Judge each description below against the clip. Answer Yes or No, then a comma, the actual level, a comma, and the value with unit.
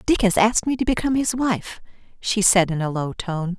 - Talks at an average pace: No, fast, 235 wpm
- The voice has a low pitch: No, high, 205 Hz